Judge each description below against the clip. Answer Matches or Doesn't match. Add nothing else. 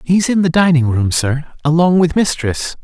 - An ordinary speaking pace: Matches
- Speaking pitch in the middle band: Matches